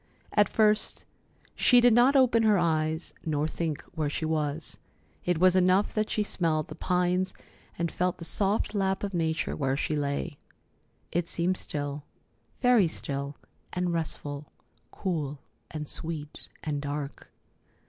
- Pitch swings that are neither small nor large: Yes, average, 4.2 semitones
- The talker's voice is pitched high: No, medium, 165 Hz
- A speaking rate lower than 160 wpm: Yes, average, 145 wpm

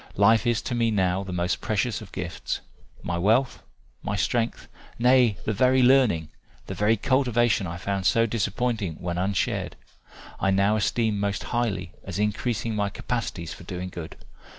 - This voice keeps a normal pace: Yes, average, 160 wpm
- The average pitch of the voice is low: Yes, low, 105 Hz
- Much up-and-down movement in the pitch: No, average, 3.8 semitones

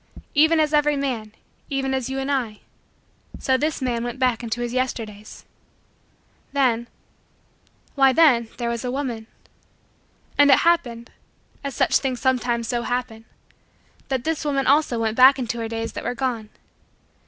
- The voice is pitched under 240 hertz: No, very high, 255 Hz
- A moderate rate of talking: Yes, average, 155 wpm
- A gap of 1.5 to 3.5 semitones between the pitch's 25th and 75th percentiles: Yes, average, 2.7 semitones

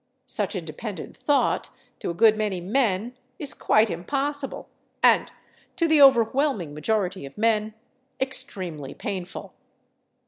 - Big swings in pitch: Yes, wide, 6.4 semitones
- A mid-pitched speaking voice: No, high, 215 Hz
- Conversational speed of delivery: No, slow, 115 wpm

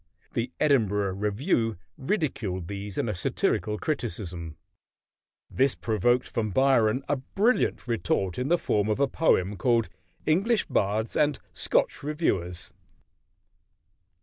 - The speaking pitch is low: Yes, low, 115 Hz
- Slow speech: Yes, slow, 120 wpm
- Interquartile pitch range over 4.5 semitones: Yes, wide, 5.5 semitones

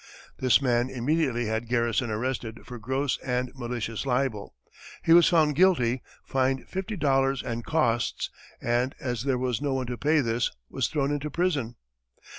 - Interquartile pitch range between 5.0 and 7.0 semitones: No, average, 3.0 semitones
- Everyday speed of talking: Yes, average, 160 wpm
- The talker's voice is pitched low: Yes, low, 130 Hz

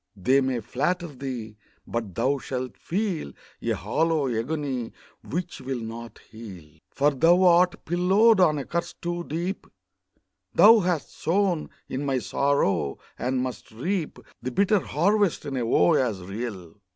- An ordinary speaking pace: Yes, average, 145 wpm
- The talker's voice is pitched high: No, medium, 140 Hz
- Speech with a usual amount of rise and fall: No, wide, 6.8 semitones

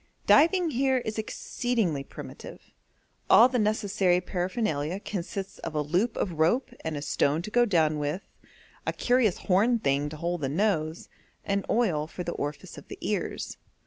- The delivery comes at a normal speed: Yes, average, 165 wpm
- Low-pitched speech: No, medium, 185 Hz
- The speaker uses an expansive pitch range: Yes, wide, 6.3 semitones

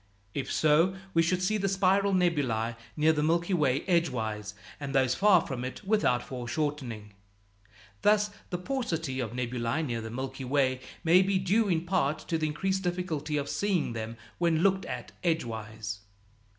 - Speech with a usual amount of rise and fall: No, wide, 6.5 semitones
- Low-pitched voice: No, medium, 155 Hz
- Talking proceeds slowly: No, average, 165 wpm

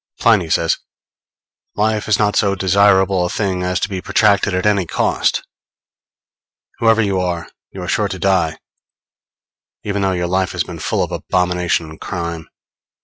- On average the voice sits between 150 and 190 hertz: No, very low, 95 Hz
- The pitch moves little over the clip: Yes, narrow, 2.3 semitones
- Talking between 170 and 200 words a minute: No, average, 160 wpm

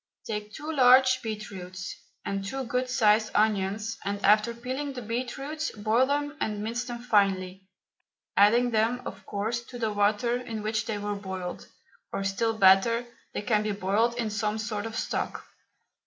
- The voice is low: No, high, 220 Hz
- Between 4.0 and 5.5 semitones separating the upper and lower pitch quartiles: No, average, 2.9 semitones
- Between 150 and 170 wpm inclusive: Yes, average, 165 wpm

